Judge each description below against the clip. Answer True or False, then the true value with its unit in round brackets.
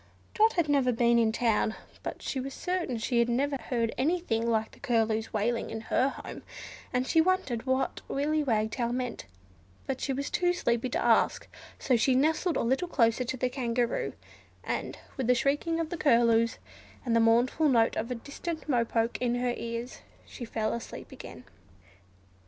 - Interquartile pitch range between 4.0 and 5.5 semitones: False (3.4 semitones)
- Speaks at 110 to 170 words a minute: False (185 wpm)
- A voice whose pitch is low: False (245 Hz)